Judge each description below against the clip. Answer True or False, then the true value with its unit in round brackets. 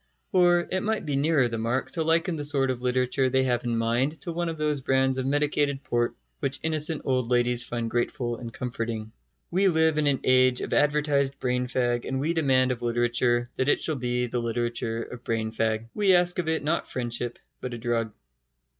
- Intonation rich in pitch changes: False (3.9 semitones)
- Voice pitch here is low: True (130 Hz)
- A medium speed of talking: False (210 wpm)